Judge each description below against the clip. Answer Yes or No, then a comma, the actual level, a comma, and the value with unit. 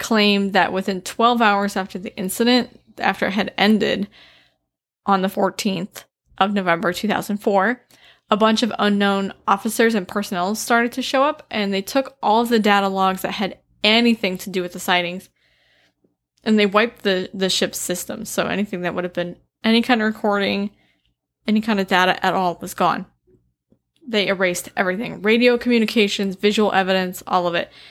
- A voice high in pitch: Yes, high, 200 Hz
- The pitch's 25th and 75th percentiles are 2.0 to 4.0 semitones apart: Yes, average, 2.8 semitones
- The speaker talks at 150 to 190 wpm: Yes, average, 170 wpm